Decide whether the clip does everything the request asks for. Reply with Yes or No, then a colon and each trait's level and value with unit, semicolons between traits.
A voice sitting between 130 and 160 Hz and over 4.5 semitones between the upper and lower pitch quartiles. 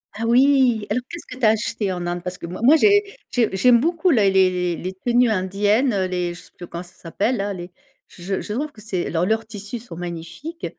No: high, 205 Hz; wide, 5.4 semitones